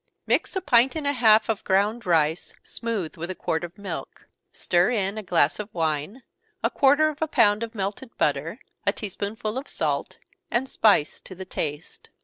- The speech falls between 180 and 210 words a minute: Yes, average, 195 wpm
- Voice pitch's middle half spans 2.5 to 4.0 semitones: No, average, 5.3 semitones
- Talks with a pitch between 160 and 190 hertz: No, high, 210 Hz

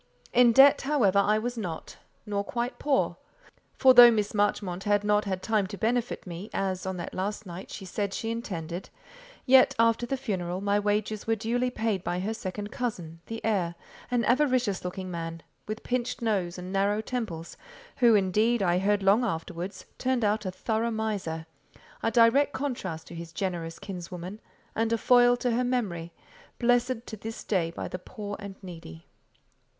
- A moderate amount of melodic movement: Yes, average, 4.2 semitones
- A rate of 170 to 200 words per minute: Yes, average, 175 wpm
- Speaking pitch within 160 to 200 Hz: No, high, 210 Hz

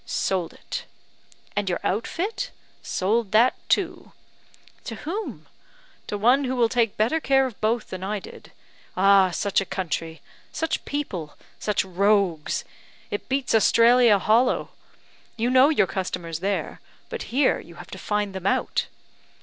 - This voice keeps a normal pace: Yes, average, 145 wpm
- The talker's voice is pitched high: Yes, high, 210 Hz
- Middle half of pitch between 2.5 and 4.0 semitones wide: No, average, 4.9 semitones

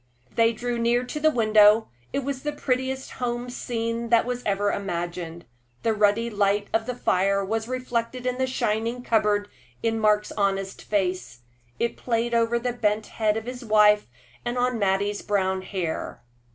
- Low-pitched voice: No, high, 225 Hz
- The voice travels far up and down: No, average, 3.1 semitones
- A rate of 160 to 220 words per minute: Yes, average, 165 wpm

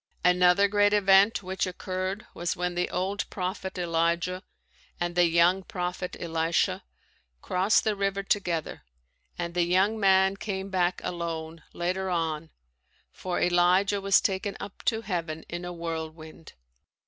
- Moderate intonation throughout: No, narrow, 2.1 semitones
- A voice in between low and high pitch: Yes, medium, 180 Hz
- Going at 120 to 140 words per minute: Yes, slow, 135 wpm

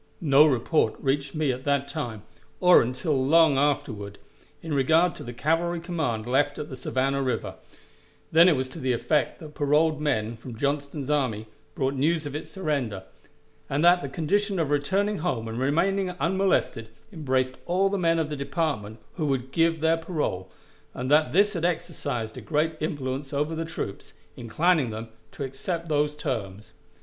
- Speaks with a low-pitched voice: No, medium, 145 Hz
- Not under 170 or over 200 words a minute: Yes, average, 175 wpm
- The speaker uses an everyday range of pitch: Yes, average, 4.1 semitones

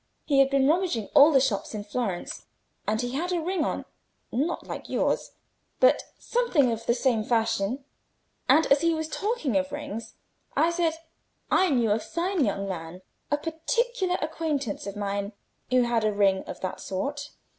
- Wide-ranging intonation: Yes, wide, 6.9 semitones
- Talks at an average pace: Yes, average, 170 wpm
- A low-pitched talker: No, very high, 270 Hz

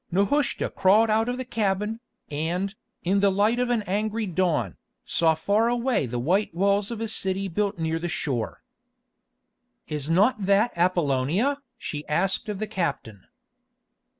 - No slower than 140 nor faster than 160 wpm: Yes, average, 150 wpm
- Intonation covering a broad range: No, average, 4.7 semitones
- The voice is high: Yes, high, 195 Hz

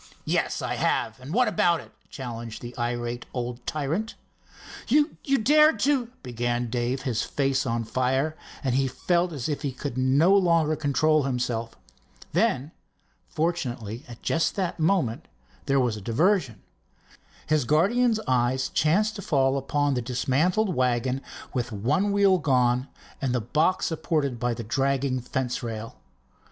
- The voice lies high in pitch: No, low, 135 Hz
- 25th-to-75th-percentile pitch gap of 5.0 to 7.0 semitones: Yes, wide, 5.5 semitones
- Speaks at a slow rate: No, average, 145 wpm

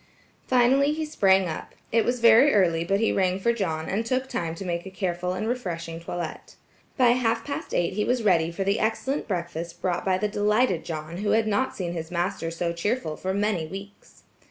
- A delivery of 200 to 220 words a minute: Yes, fast, 205 wpm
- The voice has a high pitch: Yes, high, 195 Hz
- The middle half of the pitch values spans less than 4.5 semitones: No, average, 4.8 semitones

